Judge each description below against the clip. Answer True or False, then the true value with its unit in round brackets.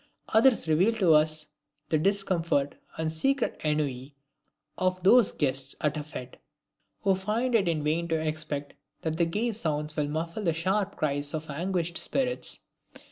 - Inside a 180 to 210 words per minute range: False (155 wpm)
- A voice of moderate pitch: True (160 Hz)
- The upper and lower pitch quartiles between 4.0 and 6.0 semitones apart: True (4.3 semitones)